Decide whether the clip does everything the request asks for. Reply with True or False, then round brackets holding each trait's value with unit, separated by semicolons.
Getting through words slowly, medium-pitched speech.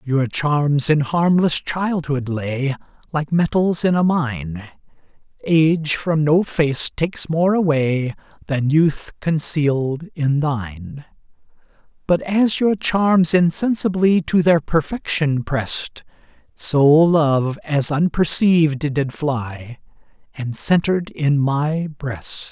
True (115 wpm; 155 Hz)